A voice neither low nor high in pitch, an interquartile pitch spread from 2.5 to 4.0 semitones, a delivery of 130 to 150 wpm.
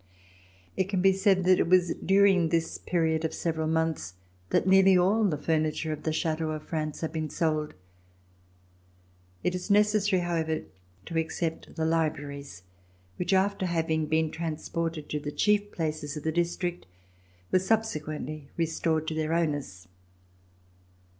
Yes: medium, 165 Hz; average, 2.8 semitones; average, 145 wpm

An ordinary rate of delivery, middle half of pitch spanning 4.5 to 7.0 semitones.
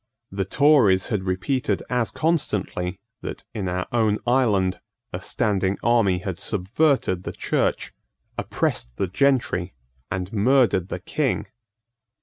No: slow, 125 wpm; average, 5.0 semitones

